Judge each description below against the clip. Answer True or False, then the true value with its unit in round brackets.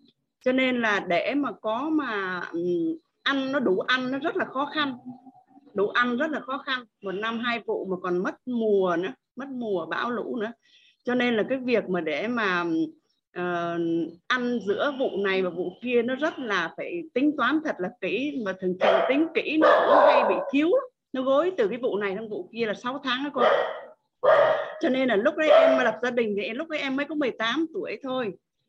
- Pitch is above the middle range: True (255 Hz)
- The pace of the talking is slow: False (220 wpm)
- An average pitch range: False (6.5 semitones)